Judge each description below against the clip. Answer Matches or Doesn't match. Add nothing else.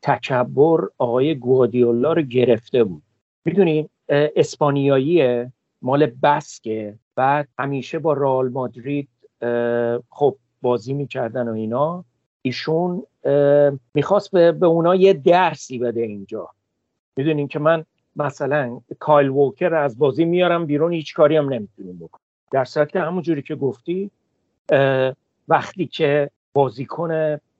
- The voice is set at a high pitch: Doesn't match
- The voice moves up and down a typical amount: Matches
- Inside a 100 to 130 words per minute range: Matches